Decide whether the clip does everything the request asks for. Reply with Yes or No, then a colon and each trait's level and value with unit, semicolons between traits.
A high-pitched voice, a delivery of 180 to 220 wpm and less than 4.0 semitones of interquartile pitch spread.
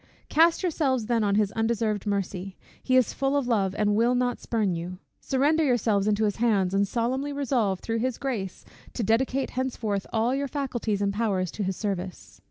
No: high, 225 Hz; average, 185 wpm; average, 4.4 semitones